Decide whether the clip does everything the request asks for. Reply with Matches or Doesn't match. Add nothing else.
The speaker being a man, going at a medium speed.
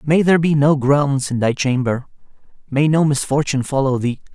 Matches